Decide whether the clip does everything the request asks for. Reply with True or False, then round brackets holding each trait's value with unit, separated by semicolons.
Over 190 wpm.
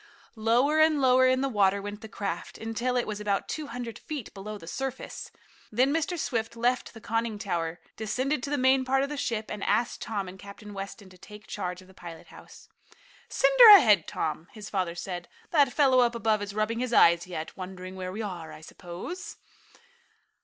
True (205 wpm)